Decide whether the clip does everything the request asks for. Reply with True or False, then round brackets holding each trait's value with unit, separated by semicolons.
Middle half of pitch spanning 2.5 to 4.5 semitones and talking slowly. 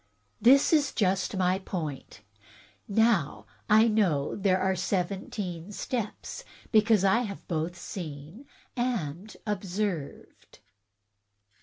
True (4.0 semitones; 105 wpm)